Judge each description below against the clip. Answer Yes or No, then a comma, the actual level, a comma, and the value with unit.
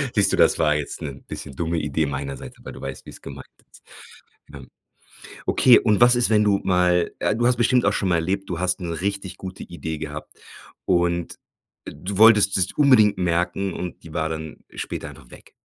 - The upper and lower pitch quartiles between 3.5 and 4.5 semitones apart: Yes, average, 4.2 semitones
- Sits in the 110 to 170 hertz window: No, very low, 90 Hz